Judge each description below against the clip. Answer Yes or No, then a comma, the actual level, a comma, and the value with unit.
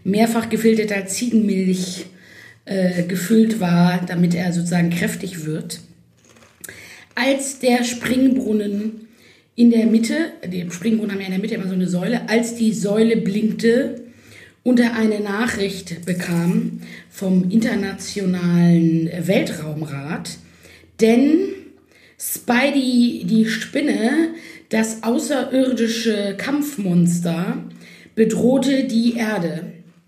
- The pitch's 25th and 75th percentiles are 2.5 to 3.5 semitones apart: No, average, 4.8 semitones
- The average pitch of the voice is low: No, high, 215 Hz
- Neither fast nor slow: No, slow, 100 wpm